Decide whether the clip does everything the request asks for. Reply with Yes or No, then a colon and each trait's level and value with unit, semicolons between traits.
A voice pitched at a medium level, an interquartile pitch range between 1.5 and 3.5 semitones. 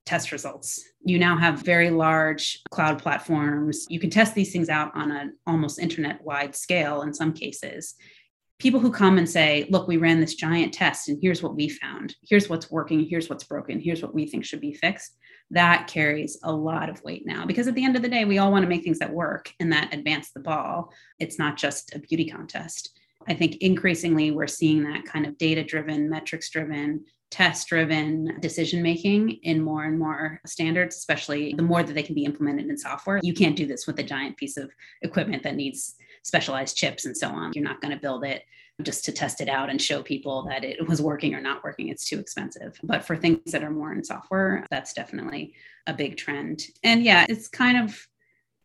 Yes: medium, 160 Hz; narrow, 2.5 semitones